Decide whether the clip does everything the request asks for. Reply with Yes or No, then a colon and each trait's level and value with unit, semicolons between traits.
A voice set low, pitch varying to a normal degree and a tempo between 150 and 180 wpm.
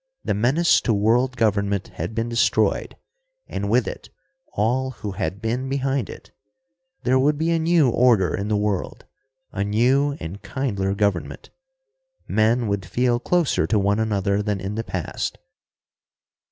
Yes: low, 110 Hz; average, 4.5 semitones; average, 155 wpm